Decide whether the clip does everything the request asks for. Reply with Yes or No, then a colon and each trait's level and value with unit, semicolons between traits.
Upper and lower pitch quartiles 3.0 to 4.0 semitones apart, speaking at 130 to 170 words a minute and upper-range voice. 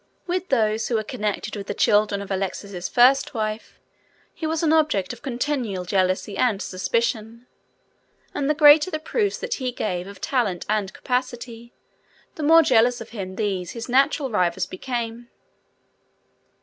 No: average, 5.2 semitones; average, 155 wpm; high, 230 Hz